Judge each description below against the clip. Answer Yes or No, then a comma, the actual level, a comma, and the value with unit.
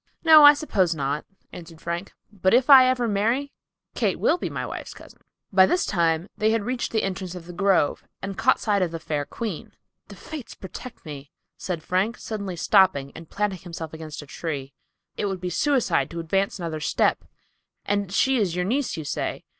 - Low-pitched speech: No, high, 190 Hz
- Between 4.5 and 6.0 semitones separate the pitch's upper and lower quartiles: Yes, average, 5.2 semitones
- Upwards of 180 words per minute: Yes, average, 195 wpm